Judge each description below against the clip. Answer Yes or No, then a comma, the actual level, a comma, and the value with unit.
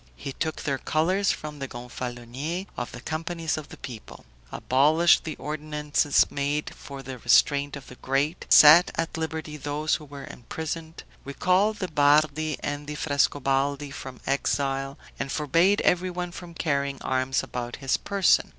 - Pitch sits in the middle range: Yes, medium, 145 Hz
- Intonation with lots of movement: No, average, 2.8 semitones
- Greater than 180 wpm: No, average, 150 wpm